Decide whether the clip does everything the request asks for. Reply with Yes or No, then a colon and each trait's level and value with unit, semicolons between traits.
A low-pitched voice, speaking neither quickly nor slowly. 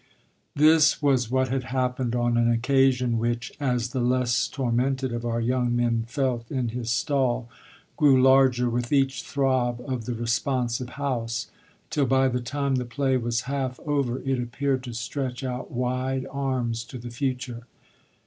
Yes: low, 125 Hz; average, 160 wpm